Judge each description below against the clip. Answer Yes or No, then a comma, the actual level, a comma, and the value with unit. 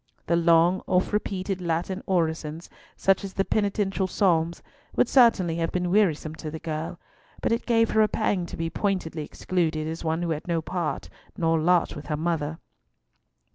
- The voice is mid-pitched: Yes, medium, 170 Hz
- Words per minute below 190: Yes, average, 175 wpm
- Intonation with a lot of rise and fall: No, average, 3.0 semitones